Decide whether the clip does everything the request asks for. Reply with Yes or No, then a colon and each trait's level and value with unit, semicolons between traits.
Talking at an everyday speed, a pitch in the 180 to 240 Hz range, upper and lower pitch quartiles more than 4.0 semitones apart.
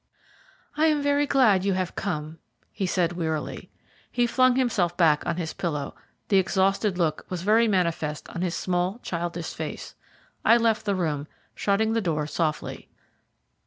Yes: average, 160 wpm; medium, 185 Hz; average, 4.7 semitones